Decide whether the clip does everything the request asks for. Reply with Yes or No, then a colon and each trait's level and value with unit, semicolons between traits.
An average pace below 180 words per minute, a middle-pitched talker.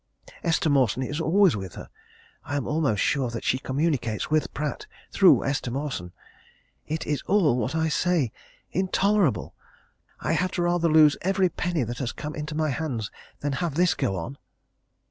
Yes: average, 165 wpm; medium, 150 Hz